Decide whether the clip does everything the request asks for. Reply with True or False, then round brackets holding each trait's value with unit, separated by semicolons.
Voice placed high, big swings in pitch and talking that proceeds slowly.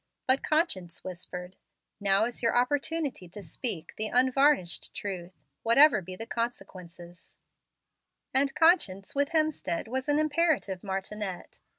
True (225 Hz; 7.3 semitones; 120 wpm)